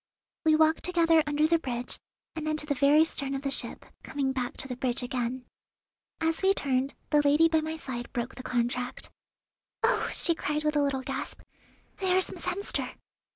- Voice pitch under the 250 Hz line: No, very high, 290 Hz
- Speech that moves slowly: No, average, 200 wpm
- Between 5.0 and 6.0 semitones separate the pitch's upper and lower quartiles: No, average, 3.7 semitones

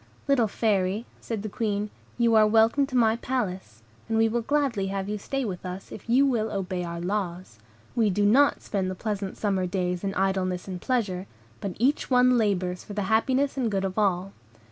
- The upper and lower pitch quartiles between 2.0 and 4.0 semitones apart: Yes, average, 3.7 semitones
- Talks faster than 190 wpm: Yes, average, 200 wpm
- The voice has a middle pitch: No, high, 205 Hz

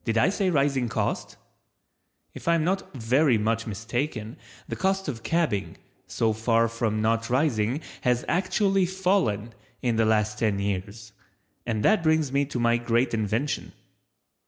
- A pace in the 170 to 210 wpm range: No, average, 155 wpm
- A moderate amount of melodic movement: No, wide, 5.8 semitones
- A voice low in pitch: Yes, low, 120 Hz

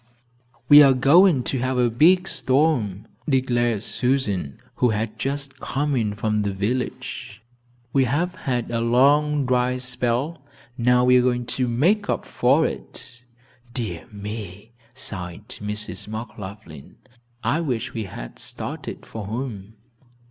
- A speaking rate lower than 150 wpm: Yes, slow, 135 wpm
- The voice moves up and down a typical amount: Yes, average, 4.1 semitones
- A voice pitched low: Yes, low, 125 Hz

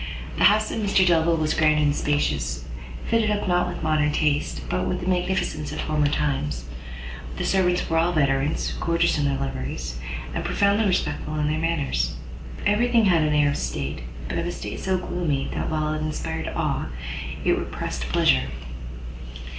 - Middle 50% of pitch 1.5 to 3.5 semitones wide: No, average, 4.4 semitones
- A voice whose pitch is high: No, medium, 155 Hz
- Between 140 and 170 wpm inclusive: No, average, 180 wpm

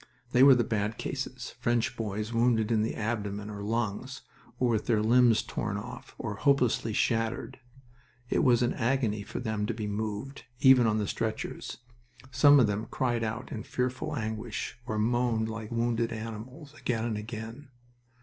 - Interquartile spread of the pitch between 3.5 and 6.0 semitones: No, narrow, 2.4 semitones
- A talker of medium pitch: No, low, 115 Hz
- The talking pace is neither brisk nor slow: Yes, average, 170 wpm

